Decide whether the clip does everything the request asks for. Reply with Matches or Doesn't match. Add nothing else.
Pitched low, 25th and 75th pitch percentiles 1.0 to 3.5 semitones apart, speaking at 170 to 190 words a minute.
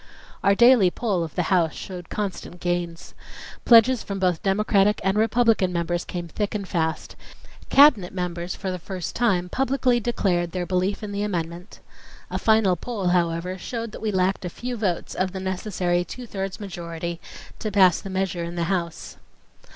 Doesn't match